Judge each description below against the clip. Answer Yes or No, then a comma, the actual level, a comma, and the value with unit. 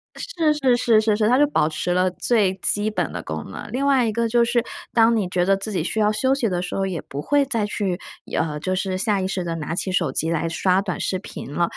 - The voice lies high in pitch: Yes, high, 195 Hz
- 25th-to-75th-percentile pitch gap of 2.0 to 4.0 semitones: No, average, 4.7 semitones